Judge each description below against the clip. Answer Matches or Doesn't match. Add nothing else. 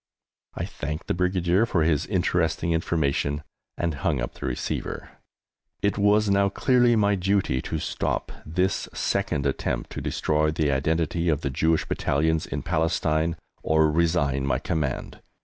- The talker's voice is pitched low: Matches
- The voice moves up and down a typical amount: Matches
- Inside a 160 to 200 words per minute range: Doesn't match